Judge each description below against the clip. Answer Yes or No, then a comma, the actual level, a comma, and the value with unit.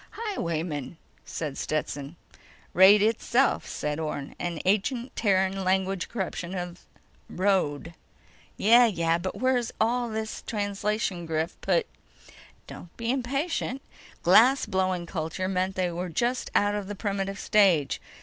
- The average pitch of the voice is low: No, high, 190 Hz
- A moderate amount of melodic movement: Yes, average, 4.4 semitones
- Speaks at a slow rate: Yes, slow, 125 wpm